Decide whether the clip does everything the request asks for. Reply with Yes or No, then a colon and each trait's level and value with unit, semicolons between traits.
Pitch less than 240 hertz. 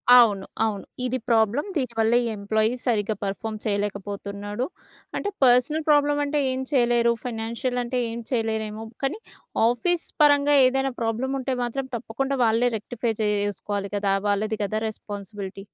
Yes: high, 225 Hz